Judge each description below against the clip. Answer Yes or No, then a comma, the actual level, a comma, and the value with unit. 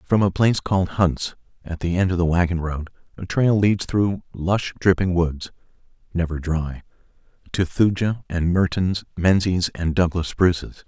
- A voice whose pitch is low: Yes, very low, 90 Hz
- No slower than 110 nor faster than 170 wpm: Yes, average, 160 wpm